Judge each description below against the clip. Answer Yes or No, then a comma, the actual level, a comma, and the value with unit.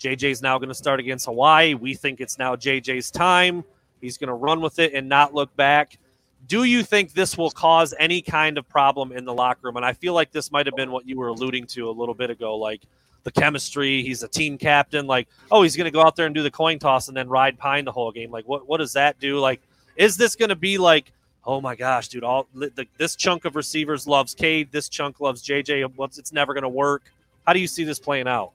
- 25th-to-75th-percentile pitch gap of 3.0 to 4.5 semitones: Yes, average, 3.3 semitones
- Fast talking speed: Yes, fast, 255 wpm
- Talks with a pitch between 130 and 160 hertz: Yes, medium, 140 Hz